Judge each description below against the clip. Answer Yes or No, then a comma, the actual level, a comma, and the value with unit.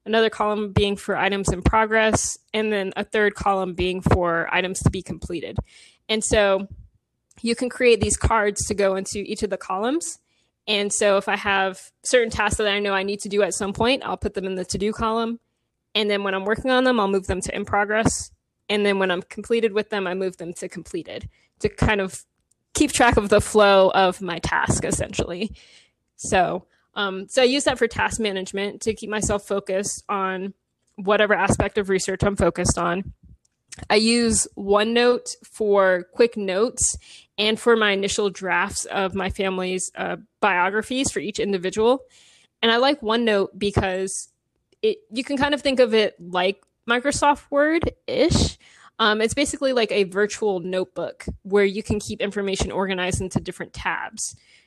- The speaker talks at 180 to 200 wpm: Yes, average, 185 wpm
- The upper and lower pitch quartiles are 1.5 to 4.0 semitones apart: Yes, average, 2.9 semitones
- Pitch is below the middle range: No, high, 205 Hz